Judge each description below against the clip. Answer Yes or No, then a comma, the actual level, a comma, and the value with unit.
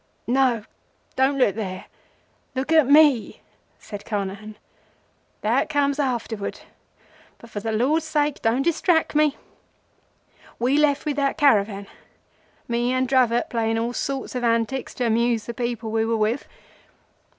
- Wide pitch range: No, average, 3.9 semitones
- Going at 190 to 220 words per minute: No, average, 140 wpm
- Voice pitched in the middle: No, high, 245 Hz